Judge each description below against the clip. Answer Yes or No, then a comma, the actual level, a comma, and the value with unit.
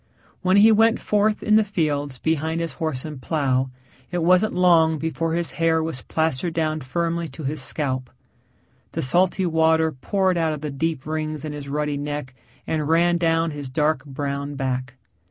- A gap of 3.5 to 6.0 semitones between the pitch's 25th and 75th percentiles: No, average, 2.9 semitones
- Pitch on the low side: No, medium, 160 Hz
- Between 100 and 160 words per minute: No, average, 175 wpm